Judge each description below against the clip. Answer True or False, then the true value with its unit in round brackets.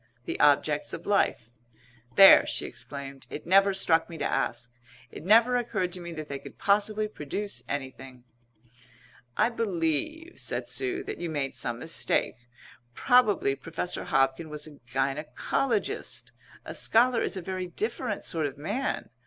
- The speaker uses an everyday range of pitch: False (7.0 semitones)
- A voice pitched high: False (170 Hz)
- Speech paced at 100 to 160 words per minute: True (150 wpm)